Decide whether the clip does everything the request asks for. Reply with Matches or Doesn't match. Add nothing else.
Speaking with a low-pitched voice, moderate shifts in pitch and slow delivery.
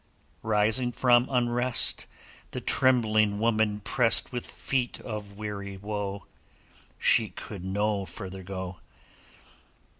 Matches